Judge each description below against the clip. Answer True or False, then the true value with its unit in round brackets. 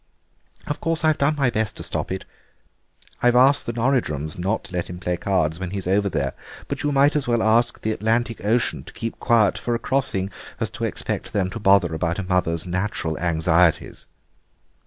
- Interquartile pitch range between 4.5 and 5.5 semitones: True (5.2 semitones)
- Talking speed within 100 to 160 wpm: False (195 wpm)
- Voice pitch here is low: True (100 Hz)